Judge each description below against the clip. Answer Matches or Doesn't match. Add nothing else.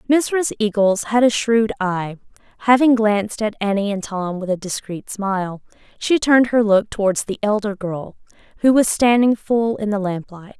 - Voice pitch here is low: Doesn't match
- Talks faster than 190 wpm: Doesn't match